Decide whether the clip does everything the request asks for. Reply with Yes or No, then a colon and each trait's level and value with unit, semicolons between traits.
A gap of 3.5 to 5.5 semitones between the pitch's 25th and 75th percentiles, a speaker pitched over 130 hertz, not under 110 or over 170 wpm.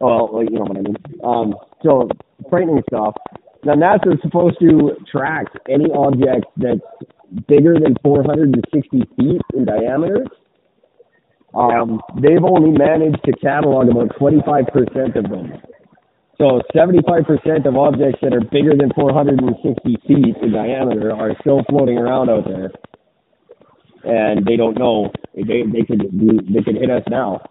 Yes: average, 4.2 semitones; medium, 140 Hz; average, 165 wpm